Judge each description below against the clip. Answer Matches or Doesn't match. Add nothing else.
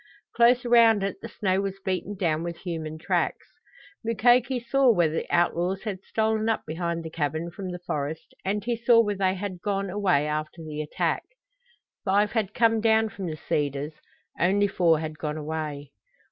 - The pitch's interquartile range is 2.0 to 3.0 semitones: Doesn't match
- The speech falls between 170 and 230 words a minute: Matches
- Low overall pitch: Doesn't match